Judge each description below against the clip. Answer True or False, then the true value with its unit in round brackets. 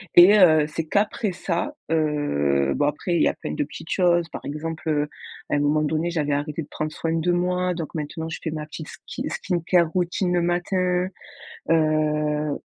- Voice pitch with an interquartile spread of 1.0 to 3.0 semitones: True (2.7 semitones)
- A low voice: False (160 Hz)